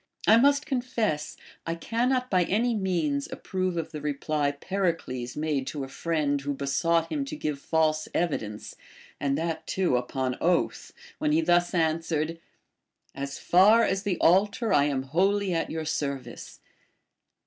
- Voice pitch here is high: No, medium, 165 Hz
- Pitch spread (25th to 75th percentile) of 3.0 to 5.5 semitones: Yes, average, 5.0 semitones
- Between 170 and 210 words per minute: No, average, 155 wpm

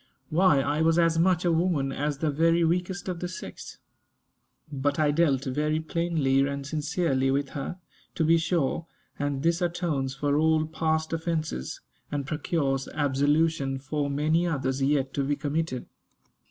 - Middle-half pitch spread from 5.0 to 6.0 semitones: No, average, 3.1 semitones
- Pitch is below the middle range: No, medium, 150 Hz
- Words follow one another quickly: No, average, 155 wpm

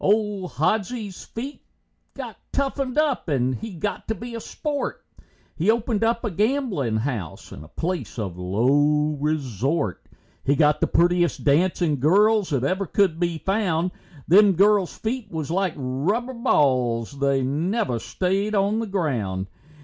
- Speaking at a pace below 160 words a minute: Yes, average, 150 wpm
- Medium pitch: Yes, medium, 175 Hz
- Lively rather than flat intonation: Yes, wide, 7.3 semitones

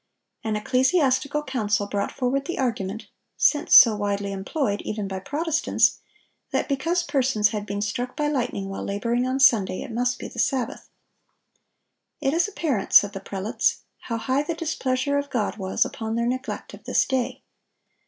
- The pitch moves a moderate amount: Yes, average, 4.8 semitones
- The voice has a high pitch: Yes, high, 245 Hz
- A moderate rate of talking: Yes, average, 165 wpm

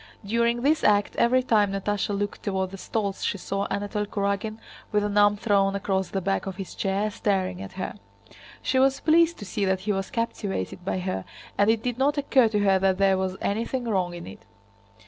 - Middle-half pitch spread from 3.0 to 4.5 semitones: No, narrow, 2.6 semitones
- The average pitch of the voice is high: Yes, high, 205 Hz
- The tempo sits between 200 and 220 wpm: Yes, fast, 205 wpm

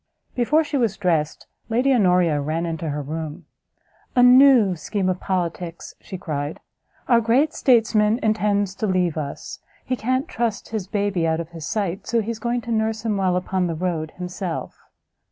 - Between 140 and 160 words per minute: No, average, 175 wpm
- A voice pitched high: Yes, high, 195 Hz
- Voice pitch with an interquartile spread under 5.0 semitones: No, average, 5.3 semitones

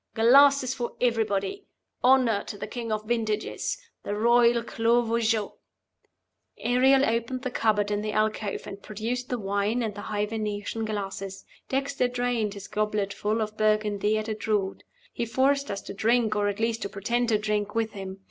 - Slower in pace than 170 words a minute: No, average, 175 wpm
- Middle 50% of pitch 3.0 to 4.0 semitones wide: No, narrow, 2.5 semitones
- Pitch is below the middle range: No, high, 220 Hz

